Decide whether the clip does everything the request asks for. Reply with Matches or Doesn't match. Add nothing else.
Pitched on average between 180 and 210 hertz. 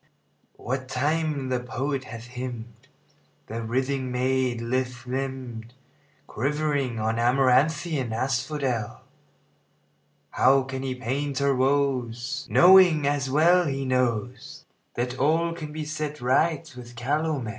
Doesn't match